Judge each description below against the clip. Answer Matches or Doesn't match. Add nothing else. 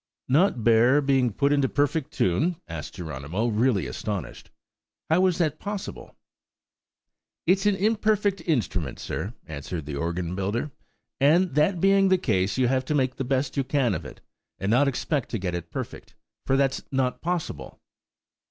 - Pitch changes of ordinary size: Doesn't match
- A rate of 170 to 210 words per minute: Doesn't match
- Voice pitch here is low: Matches